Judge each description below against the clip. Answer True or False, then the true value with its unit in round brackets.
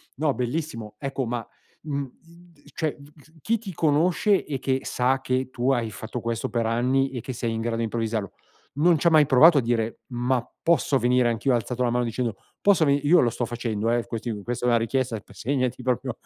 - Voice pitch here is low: True (125 Hz)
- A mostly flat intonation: False (3.2 semitones)